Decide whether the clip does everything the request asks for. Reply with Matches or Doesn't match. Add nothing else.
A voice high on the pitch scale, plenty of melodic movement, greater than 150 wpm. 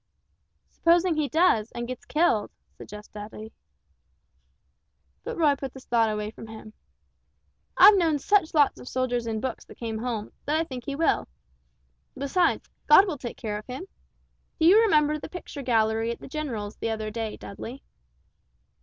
Matches